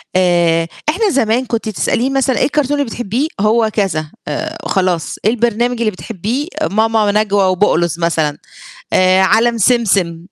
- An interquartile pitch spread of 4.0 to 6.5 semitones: Yes, average, 4.7 semitones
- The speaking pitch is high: Yes, high, 215 Hz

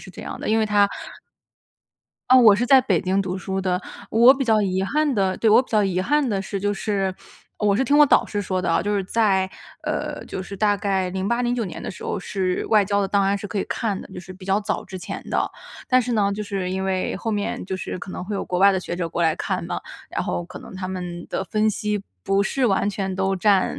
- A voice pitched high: Yes, high, 200 Hz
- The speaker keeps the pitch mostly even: Yes, narrow, 2.3 semitones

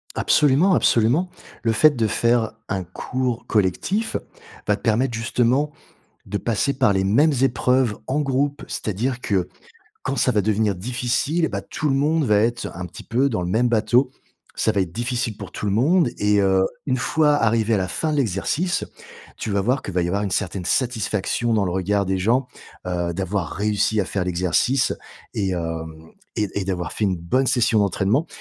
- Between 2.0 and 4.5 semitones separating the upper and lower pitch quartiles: No, average, 5.0 semitones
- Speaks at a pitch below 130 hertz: Yes, low, 110 Hz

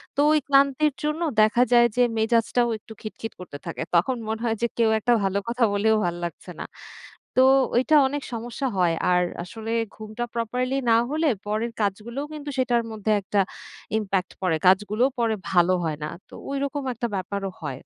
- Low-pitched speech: No, high, 225 Hz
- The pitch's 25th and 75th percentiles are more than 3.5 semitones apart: Yes, average, 4.1 semitones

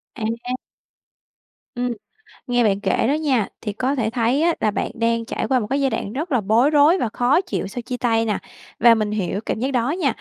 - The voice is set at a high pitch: Yes, high, 245 Hz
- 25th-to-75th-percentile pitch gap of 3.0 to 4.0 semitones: Yes, average, 3.5 semitones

